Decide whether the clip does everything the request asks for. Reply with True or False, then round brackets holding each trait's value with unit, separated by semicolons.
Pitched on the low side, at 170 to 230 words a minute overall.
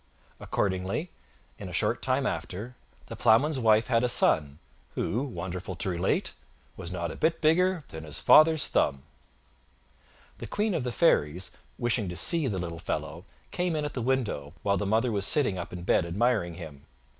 True (105 Hz; 180 wpm)